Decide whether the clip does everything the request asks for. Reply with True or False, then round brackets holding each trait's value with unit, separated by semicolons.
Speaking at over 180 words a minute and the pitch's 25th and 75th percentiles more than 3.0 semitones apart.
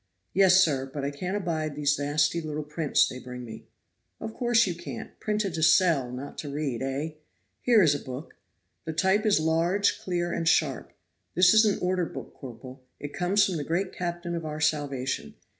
True (190 wpm; 4.2 semitones)